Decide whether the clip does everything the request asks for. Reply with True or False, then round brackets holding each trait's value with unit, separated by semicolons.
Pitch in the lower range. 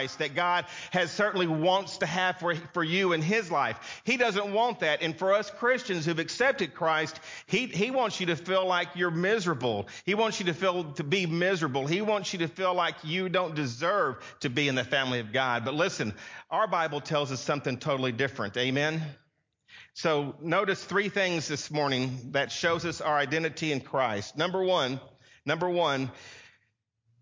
False (165 Hz)